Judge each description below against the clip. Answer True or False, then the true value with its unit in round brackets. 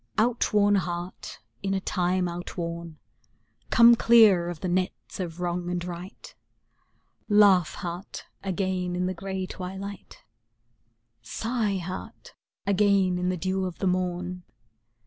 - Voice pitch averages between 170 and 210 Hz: True (185 Hz)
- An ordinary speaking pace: False (130 wpm)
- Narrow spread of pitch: True (1.9 semitones)